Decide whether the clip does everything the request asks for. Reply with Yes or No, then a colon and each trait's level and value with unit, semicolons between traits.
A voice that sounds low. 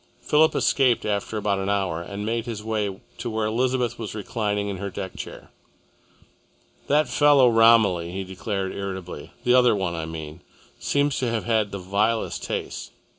Yes: low, 105 Hz